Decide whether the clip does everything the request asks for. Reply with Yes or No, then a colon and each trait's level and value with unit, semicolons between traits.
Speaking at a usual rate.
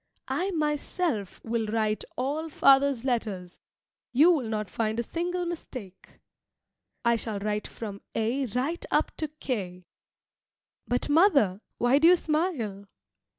No: slow, 130 wpm